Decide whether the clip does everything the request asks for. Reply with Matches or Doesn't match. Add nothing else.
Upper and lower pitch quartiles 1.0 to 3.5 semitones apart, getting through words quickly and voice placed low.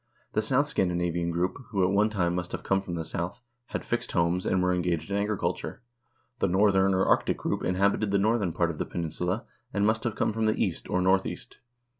Matches